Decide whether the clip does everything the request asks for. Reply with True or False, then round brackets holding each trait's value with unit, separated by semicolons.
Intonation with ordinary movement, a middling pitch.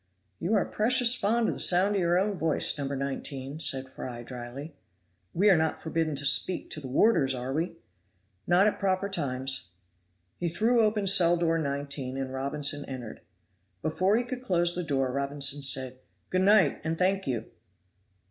False (5.9 semitones; 160 Hz)